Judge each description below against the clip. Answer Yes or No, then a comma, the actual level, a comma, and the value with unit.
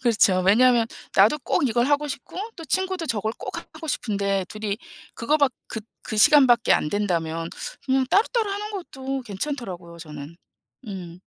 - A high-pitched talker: Yes, high, 230 Hz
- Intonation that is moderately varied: No, wide, 6.8 semitones